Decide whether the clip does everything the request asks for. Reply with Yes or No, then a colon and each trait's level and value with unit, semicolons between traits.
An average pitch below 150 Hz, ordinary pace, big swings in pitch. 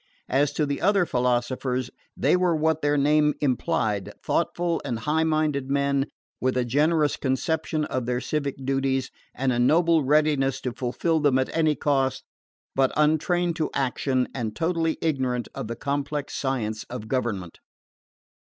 No: medium, 140 Hz; average, 150 wpm; average, 3.3 semitones